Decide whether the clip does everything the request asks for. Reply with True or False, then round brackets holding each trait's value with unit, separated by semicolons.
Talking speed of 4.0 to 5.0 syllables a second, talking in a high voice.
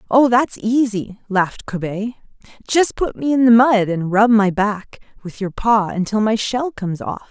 True (4.5 syllables/s; 215 Hz)